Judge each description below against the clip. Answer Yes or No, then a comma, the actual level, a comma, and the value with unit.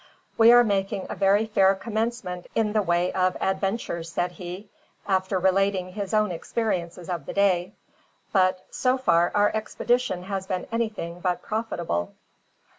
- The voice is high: Yes, high, 195 Hz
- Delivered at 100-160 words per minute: Yes, average, 150 wpm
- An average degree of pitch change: Yes, average, 3.0 semitones